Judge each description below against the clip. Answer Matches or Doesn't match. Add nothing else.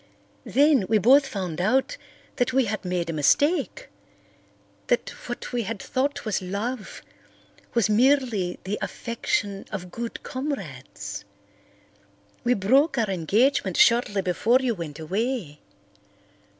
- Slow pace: Matches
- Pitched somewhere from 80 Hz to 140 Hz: Doesn't match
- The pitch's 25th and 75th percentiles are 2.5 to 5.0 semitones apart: Doesn't match